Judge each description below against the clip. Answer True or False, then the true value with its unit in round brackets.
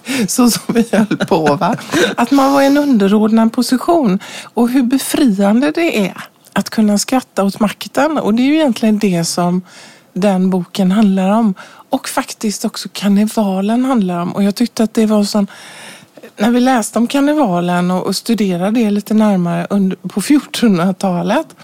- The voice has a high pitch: True (215 Hz)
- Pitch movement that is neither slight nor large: True (4.0 semitones)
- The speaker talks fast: False (160 wpm)